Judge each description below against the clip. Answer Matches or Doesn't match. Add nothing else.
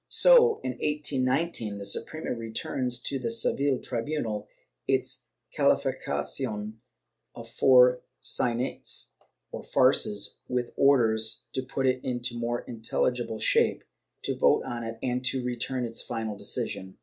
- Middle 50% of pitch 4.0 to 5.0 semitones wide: Doesn't match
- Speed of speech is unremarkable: Doesn't match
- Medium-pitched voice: Doesn't match